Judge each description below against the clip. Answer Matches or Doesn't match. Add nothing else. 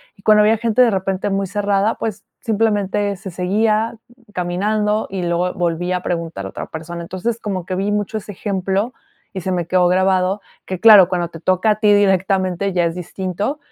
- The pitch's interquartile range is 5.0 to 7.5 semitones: Doesn't match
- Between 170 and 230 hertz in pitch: Matches